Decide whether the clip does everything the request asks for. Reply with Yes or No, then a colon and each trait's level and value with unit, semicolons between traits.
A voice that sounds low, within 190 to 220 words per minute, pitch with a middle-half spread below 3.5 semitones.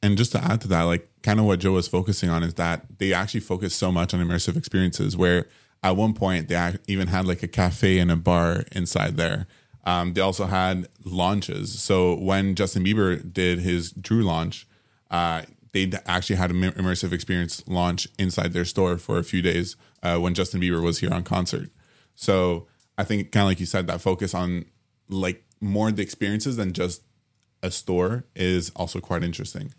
Yes: very low, 95 Hz; average, 200 wpm; narrow, 2.5 semitones